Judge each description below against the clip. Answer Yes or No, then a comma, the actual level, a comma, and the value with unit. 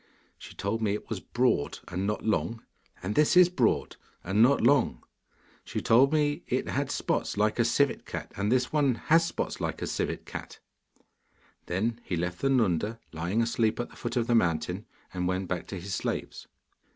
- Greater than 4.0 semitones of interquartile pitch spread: Yes, average, 5.1 semitones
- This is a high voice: No, low, 115 Hz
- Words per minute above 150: Yes, average, 190 wpm